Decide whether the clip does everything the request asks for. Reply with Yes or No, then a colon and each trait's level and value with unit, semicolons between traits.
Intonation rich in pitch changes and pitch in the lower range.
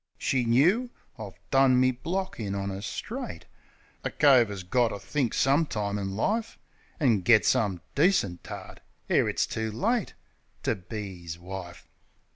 Yes: wide, 6.0 semitones; low, 110 Hz